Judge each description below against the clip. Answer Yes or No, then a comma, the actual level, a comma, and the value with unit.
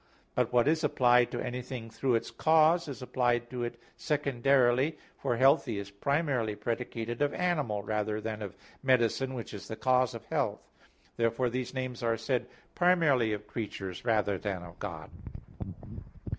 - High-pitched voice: No, low, 120 Hz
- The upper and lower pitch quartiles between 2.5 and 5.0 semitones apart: Yes, average, 3.3 semitones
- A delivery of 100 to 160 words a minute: Yes, average, 155 wpm